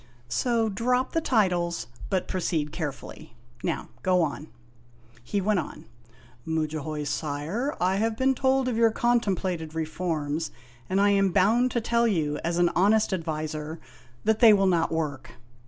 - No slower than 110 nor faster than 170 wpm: Yes, average, 160 wpm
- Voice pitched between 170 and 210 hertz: Yes, medium, 185 Hz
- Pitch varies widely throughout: Yes, wide, 5.8 semitones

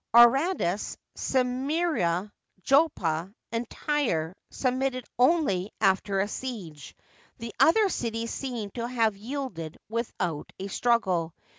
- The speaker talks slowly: Yes, slow, 110 wpm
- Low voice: No, high, 230 Hz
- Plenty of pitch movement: Yes, wide, 5.7 semitones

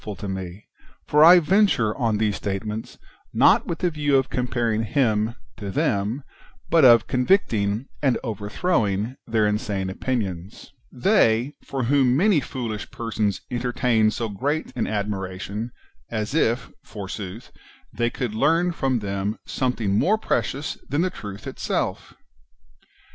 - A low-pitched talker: Yes, low, 115 Hz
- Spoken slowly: No, average, 145 wpm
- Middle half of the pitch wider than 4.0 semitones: Yes, average, 4.6 semitones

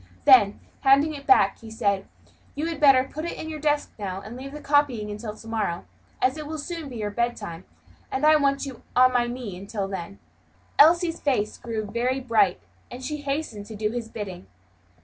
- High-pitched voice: Yes, high, 245 Hz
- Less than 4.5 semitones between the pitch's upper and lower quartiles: No, wide, 5.5 semitones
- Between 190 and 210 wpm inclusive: Yes, average, 200 wpm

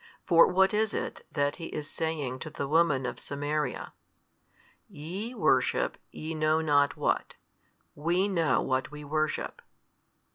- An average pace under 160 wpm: Yes, average, 140 wpm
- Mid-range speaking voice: Yes, medium, 155 Hz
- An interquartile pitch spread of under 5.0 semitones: Yes, average, 2.7 semitones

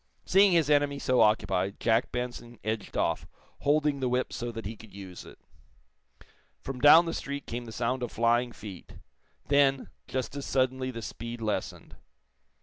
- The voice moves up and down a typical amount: Yes, average, 3.7 semitones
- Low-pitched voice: Yes, low, 125 Hz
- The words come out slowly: No, average, 165 wpm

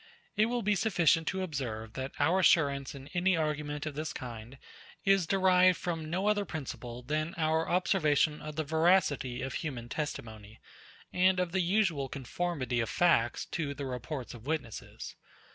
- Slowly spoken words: No, average, 160 wpm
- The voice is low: No, medium, 155 Hz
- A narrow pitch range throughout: No, average, 5.2 semitones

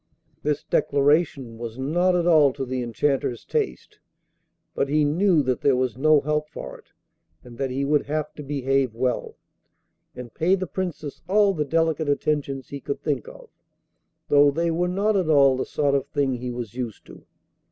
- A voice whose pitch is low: No, medium, 145 Hz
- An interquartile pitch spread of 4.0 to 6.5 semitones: No, average, 3.2 semitones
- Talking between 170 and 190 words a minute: Yes, average, 185 wpm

